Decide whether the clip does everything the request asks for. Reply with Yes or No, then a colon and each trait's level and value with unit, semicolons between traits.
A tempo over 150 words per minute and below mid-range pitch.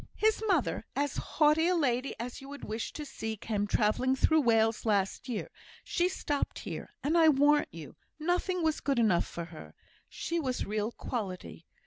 No: average, 175 wpm; very high, 260 Hz